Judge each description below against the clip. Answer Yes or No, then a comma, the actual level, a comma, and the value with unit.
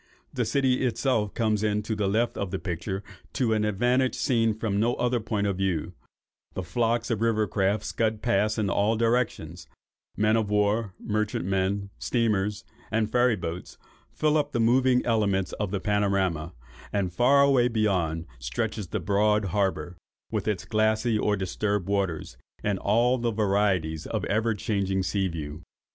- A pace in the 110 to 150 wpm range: No, average, 160 wpm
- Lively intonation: No, average, 2.9 semitones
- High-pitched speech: No, low, 105 Hz